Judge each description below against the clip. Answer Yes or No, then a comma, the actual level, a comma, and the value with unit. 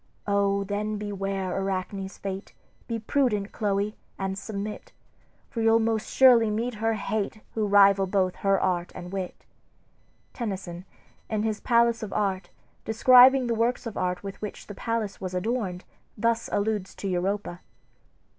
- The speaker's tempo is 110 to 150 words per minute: Yes, average, 145 wpm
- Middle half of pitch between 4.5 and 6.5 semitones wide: No, narrow, 2.5 semitones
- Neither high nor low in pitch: No, high, 205 Hz